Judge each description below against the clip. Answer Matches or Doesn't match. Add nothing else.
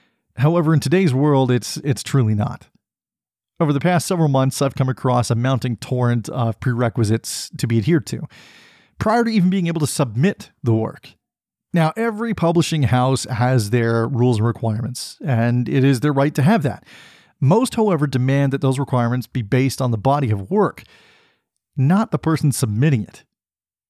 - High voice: Doesn't match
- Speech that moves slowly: Doesn't match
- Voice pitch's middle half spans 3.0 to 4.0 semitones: Doesn't match